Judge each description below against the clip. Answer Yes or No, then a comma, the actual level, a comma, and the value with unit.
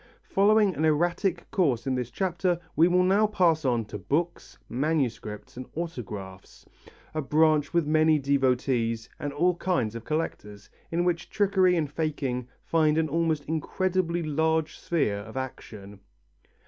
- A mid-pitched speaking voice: Yes, medium, 155 Hz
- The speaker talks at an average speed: Yes, average, 145 wpm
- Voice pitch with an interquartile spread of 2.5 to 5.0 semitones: No, wide, 5.4 semitones